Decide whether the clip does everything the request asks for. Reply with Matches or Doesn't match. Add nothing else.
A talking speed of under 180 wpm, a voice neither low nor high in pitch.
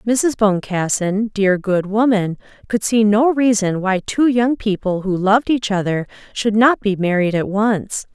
Doesn't match